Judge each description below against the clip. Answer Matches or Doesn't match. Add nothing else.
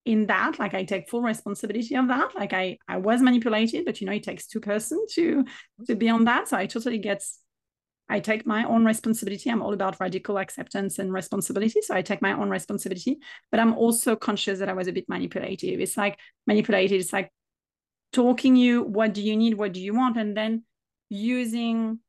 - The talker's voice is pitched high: Matches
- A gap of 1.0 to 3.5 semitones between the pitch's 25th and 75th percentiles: Matches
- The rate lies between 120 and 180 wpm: Doesn't match